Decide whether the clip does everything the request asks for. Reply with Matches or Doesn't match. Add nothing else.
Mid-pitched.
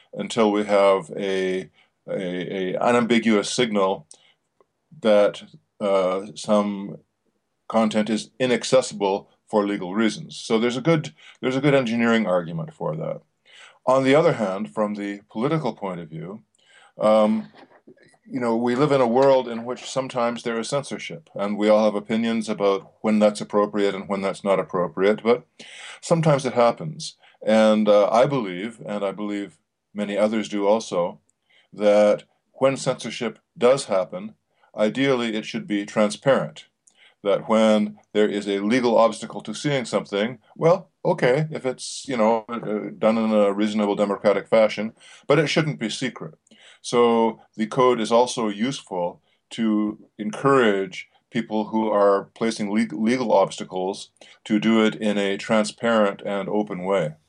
Doesn't match